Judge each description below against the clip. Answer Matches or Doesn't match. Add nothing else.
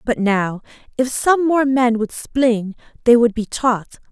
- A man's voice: Doesn't match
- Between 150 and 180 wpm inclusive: Matches